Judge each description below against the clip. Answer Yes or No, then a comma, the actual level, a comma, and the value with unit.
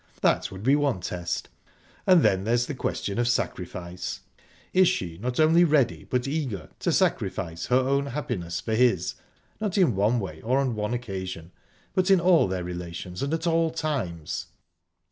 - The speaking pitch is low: Yes, low, 120 Hz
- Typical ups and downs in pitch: No, wide, 8.4 semitones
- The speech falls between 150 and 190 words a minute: Yes, average, 165 wpm